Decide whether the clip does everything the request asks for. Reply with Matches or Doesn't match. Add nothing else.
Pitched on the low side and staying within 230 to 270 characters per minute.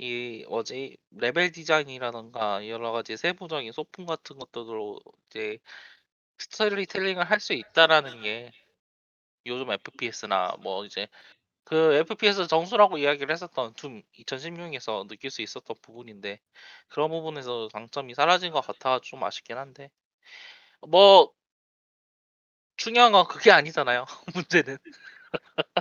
Doesn't match